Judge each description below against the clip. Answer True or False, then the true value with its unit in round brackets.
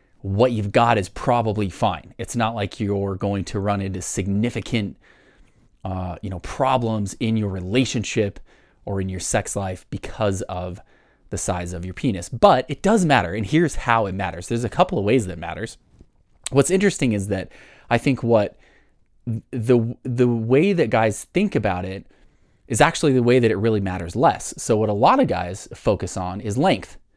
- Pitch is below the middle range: True (110 Hz)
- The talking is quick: False (190 wpm)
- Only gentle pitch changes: False (4.0 semitones)